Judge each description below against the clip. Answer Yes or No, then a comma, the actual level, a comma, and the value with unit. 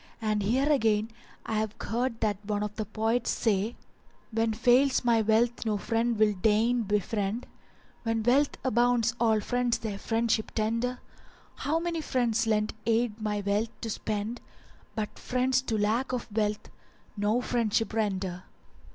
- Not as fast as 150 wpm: No, average, 155 wpm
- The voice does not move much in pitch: Yes, narrow, 2.3 semitones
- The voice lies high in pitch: Yes, high, 225 Hz